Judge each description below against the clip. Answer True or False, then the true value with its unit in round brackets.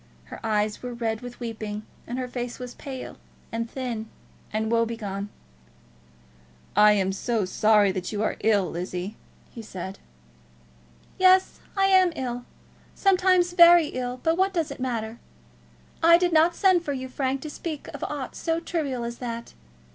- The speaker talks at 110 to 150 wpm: False (160 wpm)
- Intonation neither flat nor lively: False (6.9 semitones)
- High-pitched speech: True (245 Hz)